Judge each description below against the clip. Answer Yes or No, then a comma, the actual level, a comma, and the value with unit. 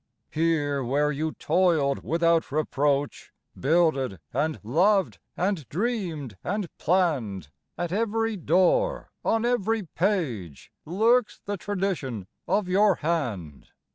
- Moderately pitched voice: Yes, medium, 165 Hz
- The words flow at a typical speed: No, slow, 110 wpm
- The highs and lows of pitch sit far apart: Yes, wide, 6.1 semitones